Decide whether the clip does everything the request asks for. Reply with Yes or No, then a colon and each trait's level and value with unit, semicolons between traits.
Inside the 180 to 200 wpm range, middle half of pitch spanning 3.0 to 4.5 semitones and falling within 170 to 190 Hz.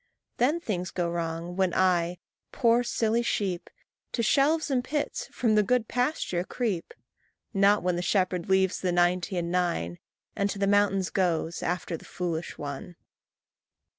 No: average, 155 wpm; average, 4.2 semitones; medium, 185 Hz